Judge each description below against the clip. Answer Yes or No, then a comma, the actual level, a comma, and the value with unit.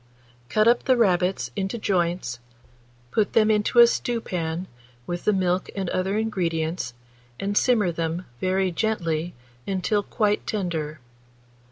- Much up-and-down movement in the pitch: No, average, 3.7 semitones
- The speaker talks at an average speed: No, slow, 130 wpm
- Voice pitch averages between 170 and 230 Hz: Yes, high, 190 Hz